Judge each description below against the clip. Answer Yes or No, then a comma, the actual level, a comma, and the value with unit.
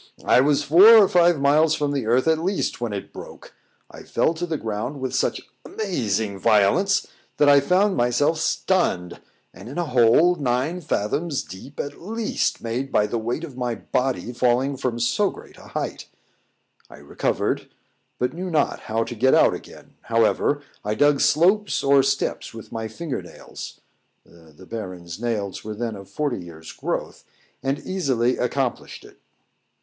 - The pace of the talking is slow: No, average, 165 wpm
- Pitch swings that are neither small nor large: No, wide, 5.8 semitones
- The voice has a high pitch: No, low, 130 Hz